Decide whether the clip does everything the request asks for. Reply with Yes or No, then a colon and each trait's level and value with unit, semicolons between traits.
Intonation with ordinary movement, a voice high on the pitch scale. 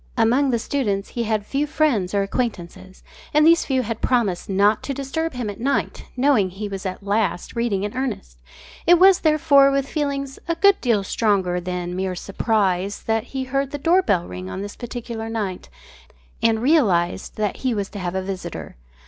No: wide, 6.1 semitones; high, 225 Hz